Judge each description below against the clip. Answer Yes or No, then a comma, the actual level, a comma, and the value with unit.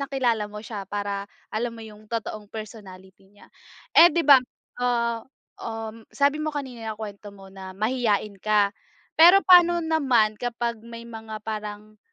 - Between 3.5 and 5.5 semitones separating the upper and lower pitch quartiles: No, average, 2.9 semitones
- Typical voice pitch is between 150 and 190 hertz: No, high, 220 Hz